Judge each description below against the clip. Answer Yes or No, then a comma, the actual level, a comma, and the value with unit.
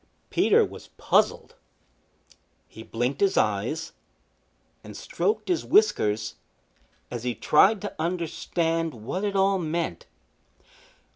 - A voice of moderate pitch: Yes, medium, 165 Hz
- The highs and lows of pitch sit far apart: Yes, wide, 8.2 semitones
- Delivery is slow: Yes, slow, 110 wpm